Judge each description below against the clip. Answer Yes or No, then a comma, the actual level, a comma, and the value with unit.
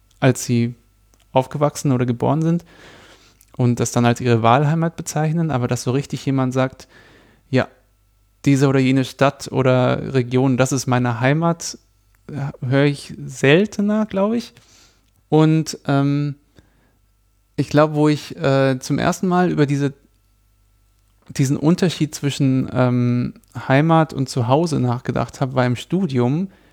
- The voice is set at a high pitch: No, low, 135 Hz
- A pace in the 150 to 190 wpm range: No, average, 130 wpm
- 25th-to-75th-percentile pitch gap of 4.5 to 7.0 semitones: No, average, 3.5 semitones